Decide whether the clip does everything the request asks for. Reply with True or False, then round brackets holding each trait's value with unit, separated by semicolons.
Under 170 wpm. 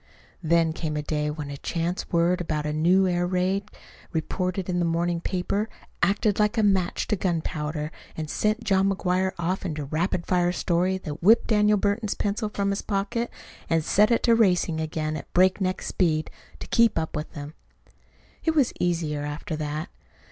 False (180 wpm)